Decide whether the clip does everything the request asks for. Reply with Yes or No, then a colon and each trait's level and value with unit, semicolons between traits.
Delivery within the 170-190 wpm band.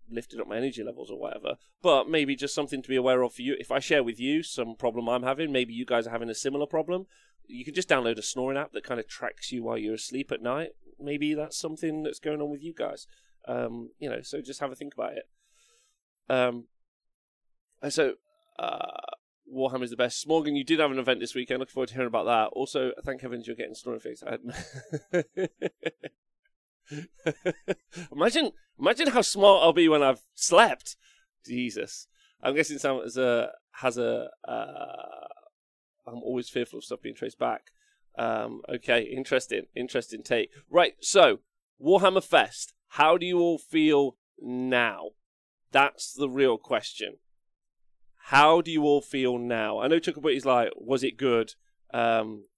Yes: average, 180 wpm